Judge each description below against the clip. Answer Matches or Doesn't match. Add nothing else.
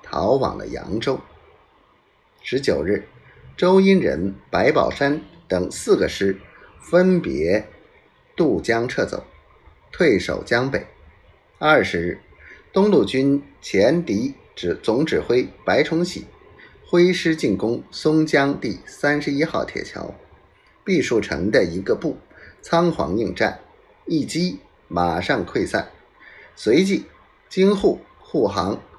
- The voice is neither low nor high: Matches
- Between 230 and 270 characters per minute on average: Doesn't match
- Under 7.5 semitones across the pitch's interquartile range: Matches